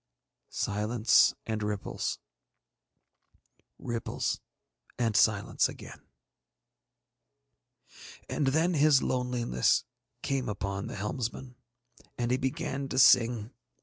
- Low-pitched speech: Yes, low, 120 Hz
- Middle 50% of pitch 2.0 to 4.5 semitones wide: Yes, average, 3.8 semitones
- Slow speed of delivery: Yes, slow, 85 wpm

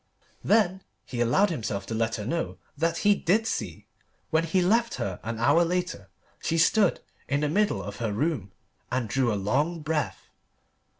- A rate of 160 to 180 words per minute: Yes, average, 175 wpm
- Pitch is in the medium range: Yes, medium, 155 Hz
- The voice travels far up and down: Yes, wide, 7.6 semitones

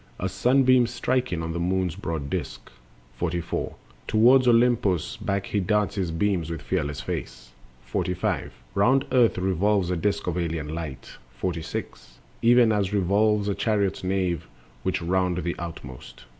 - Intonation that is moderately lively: Yes, average, 3.9 semitones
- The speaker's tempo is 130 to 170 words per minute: Yes, average, 145 wpm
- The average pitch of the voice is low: Yes, very low, 95 Hz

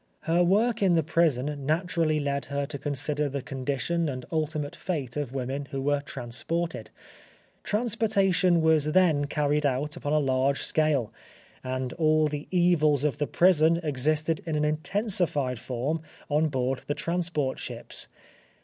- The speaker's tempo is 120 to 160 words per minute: Yes, average, 150 wpm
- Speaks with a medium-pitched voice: Yes, medium, 150 Hz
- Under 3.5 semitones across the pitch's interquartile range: Yes, average, 3.1 semitones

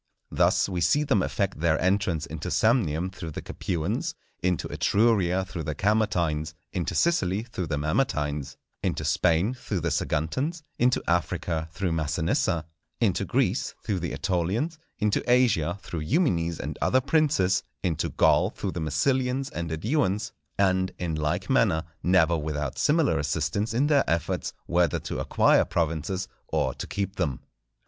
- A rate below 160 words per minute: Yes, average, 150 wpm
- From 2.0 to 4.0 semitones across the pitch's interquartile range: No, average, 5.1 semitones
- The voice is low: Yes, very low, 90 Hz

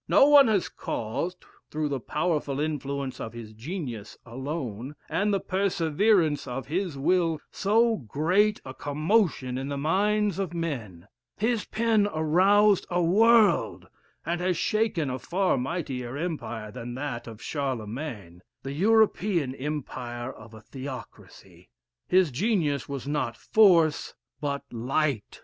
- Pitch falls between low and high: Yes, medium, 150 Hz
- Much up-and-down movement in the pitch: Yes, wide, 6.5 semitones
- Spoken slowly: Yes, slow, 130 wpm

